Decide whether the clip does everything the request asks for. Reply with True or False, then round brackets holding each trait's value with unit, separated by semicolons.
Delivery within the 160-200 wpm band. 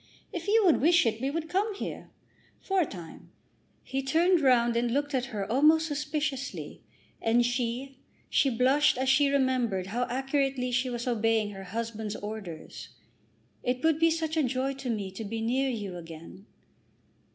True (170 wpm)